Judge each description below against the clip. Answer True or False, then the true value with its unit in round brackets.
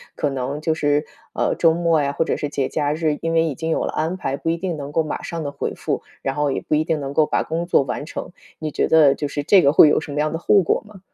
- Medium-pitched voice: True (155 Hz)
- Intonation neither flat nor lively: False (2.1 semitones)